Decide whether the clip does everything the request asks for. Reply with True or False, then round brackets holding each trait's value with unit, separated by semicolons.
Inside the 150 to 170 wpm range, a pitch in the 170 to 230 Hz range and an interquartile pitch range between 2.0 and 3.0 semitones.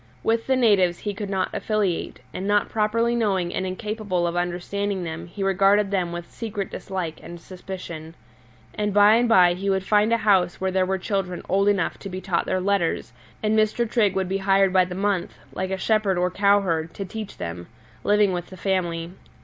False (200 wpm; 190 Hz; 2.5 semitones)